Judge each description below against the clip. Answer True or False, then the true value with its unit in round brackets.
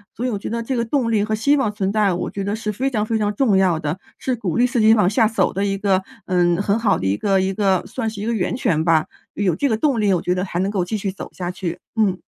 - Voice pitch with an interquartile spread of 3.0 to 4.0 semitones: True (3.3 semitones)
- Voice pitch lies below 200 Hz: False (205 Hz)